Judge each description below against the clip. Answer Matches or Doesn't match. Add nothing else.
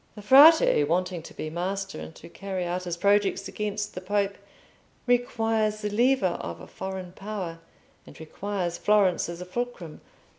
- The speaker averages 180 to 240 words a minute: Doesn't match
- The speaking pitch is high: Matches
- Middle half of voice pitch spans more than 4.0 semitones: Doesn't match